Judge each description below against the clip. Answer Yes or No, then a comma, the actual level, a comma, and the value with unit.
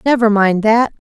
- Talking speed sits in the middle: Yes, average, 155 wpm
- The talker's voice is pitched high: Yes, high, 220 Hz